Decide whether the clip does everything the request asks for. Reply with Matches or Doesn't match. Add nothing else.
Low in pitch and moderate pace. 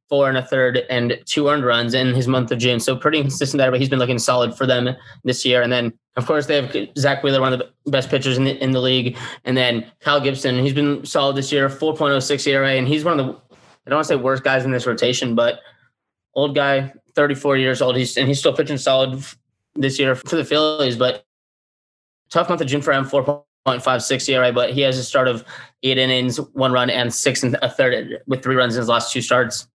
Doesn't match